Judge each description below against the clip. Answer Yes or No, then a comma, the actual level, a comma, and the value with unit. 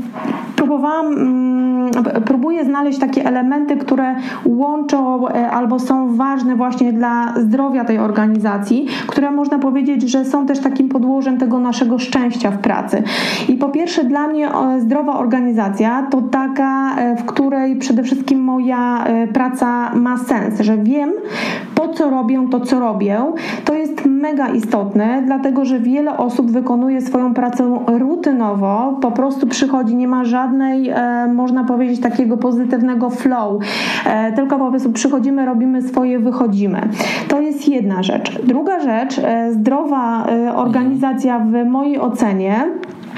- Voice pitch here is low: No, very high, 255 Hz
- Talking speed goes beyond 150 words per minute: No, average, 130 wpm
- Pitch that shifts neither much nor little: No, narrow, 2.3 semitones